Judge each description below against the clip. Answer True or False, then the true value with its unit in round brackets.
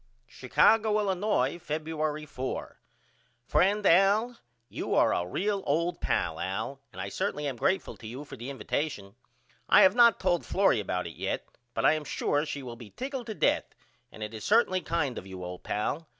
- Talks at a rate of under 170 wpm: False (185 wpm)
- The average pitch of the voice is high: False (155 Hz)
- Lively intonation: True (8.4 semitones)